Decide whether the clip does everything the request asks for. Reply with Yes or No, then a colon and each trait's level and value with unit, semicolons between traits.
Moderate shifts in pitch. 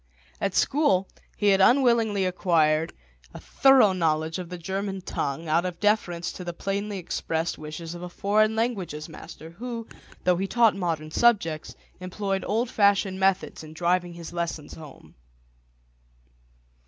Yes: average, 3.6 semitones